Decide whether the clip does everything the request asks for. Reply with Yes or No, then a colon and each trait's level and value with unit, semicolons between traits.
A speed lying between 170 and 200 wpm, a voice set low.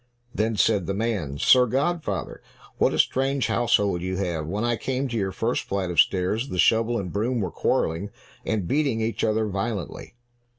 Yes: average, 180 wpm; low, 110 Hz